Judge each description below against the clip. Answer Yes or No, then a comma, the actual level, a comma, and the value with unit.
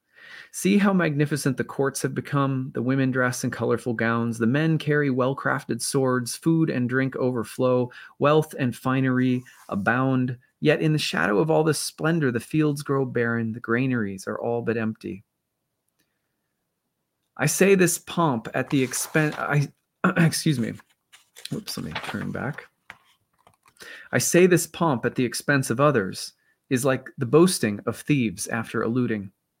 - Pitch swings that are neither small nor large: Yes, average, 4.3 semitones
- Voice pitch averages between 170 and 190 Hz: No, low, 130 Hz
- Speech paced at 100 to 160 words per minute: Yes, average, 150 wpm